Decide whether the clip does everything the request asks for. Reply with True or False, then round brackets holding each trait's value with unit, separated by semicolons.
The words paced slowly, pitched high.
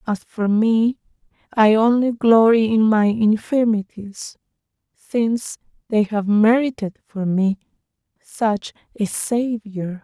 True (110 wpm; 220 Hz)